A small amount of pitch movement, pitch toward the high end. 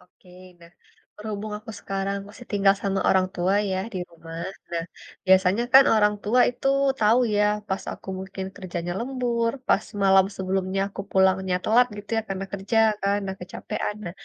Yes: narrow, 2.1 semitones; high, 195 Hz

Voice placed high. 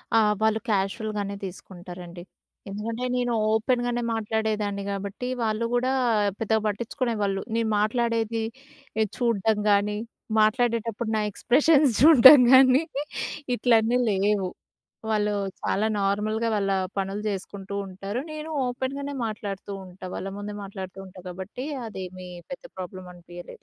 Yes: high, 215 Hz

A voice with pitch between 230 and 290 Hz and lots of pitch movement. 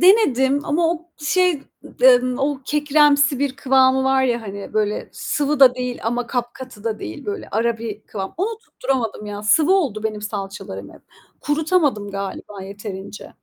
Yes: very high, 255 Hz; wide, 5.7 semitones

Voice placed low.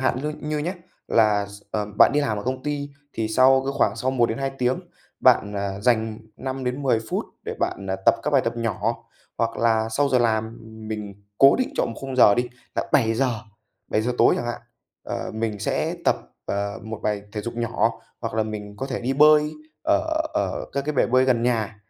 Yes: low, 115 Hz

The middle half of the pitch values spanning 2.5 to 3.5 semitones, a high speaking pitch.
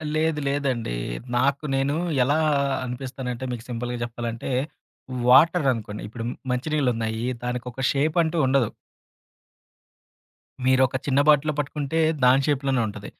No: average, 2.9 semitones; low, 130 Hz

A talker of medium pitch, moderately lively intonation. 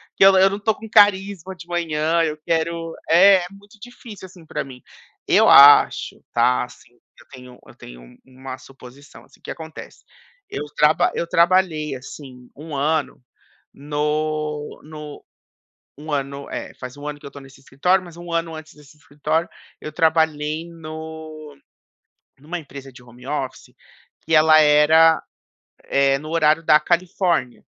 Yes: medium, 155 Hz; average, 3.1 semitones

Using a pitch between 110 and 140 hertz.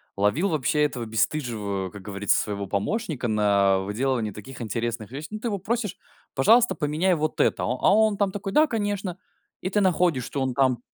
Yes: low, 135 Hz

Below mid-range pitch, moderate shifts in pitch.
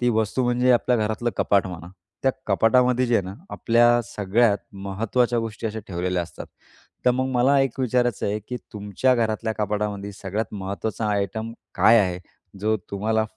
Yes: low, 110 Hz; average, 3.2 semitones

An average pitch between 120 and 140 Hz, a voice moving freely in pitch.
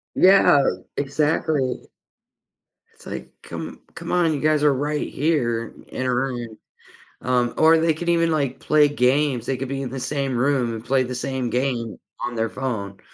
No: low, 135 Hz; average, 3.4 semitones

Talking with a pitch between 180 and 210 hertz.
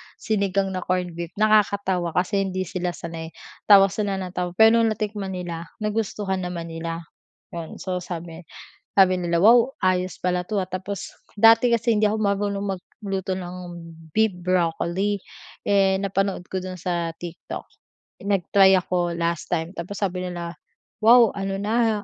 Yes: medium, 185 Hz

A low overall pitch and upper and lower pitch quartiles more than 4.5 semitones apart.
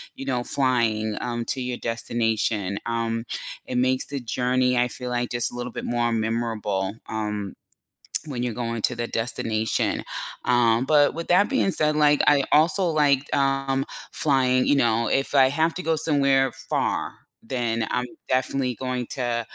No: low, 125 Hz; average, 2.8 semitones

